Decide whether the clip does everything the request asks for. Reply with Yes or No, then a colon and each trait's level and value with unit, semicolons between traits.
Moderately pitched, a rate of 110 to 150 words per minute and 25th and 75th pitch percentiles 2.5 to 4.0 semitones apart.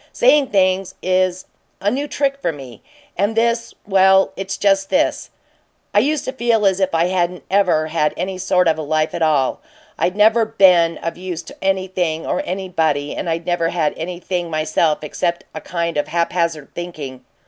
No: medium, 180 Hz; average, 180 wpm; average, 2.9 semitones